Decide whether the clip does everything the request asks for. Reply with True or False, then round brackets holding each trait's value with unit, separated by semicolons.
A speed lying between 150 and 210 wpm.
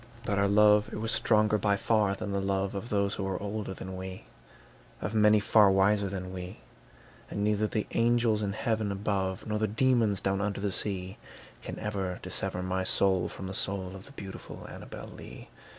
True (195 wpm)